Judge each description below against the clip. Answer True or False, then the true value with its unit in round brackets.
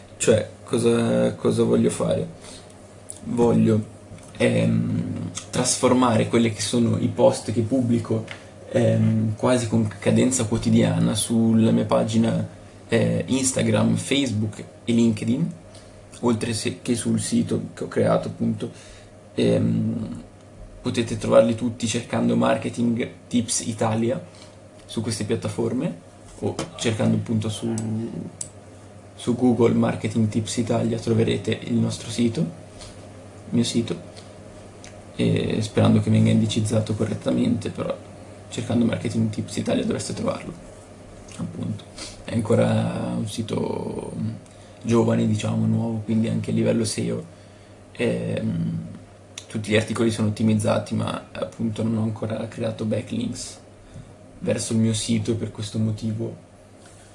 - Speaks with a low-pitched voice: True (110 Hz)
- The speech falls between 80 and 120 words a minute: True (115 wpm)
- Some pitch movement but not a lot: False (1.9 semitones)